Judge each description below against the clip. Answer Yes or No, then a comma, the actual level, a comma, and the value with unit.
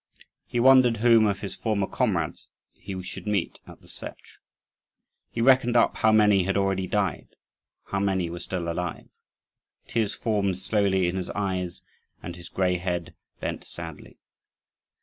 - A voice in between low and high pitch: No, very low, 95 Hz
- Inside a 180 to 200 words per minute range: No, average, 150 wpm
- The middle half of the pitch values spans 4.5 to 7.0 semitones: No, average, 3.0 semitones